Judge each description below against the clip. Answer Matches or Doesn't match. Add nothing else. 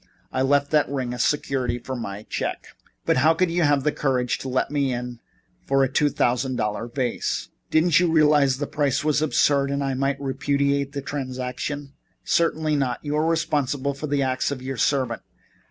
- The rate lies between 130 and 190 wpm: Doesn't match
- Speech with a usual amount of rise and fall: Doesn't match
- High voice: Doesn't match